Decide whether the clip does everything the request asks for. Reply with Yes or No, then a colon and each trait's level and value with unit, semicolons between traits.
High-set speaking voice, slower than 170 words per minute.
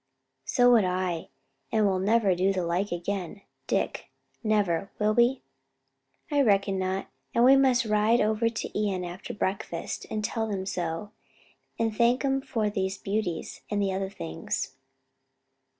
Yes: high, 205 Hz; average, 150 wpm